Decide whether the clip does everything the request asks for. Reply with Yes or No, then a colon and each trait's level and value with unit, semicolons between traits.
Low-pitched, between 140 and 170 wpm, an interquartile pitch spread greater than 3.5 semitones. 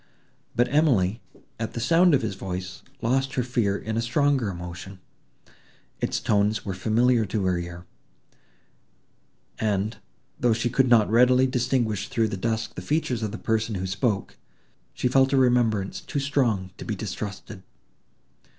Yes: low, 110 Hz; average, 155 wpm; average, 4.2 semitones